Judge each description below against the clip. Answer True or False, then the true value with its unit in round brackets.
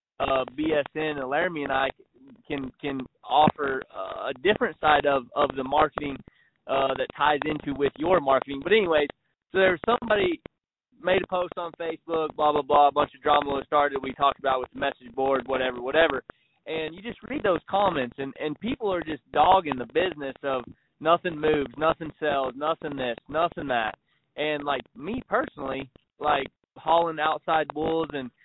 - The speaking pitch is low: False (150 Hz)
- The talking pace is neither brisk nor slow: True (180 wpm)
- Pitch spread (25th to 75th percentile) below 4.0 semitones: True (3.3 semitones)